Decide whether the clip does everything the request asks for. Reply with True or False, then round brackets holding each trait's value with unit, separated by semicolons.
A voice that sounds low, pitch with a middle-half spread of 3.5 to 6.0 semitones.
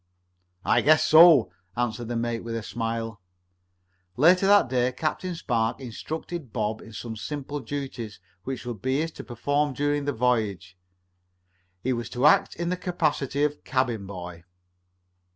True (125 Hz; 4.4 semitones)